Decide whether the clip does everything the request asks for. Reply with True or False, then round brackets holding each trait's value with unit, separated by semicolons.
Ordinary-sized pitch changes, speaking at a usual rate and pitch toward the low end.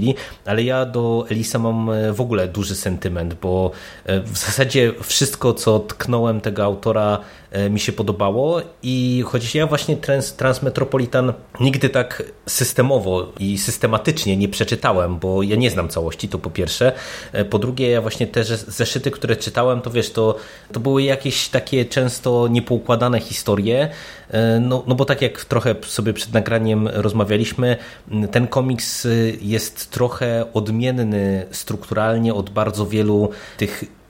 True (3.1 semitones; 135 wpm; 115 Hz)